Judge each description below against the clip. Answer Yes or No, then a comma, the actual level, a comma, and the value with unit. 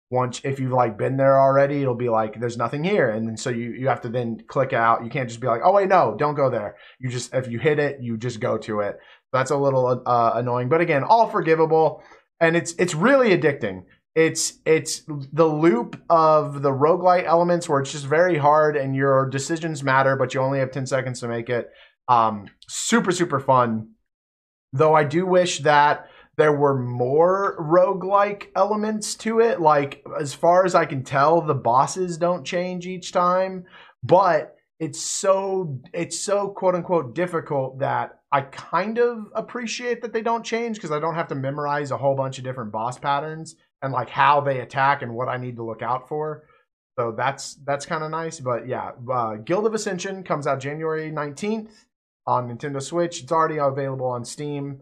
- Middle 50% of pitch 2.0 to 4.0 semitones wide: No, average, 5.2 semitones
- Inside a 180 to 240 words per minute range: Yes, average, 195 wpm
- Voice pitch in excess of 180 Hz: No, medium, 145 Hz